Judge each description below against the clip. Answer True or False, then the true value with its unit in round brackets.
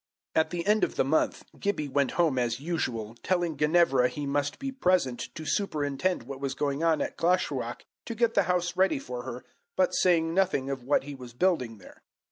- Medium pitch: True (150 Hz)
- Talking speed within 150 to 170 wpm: False (200 wpm)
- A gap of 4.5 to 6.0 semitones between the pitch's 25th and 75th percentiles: True (5.2 semitones)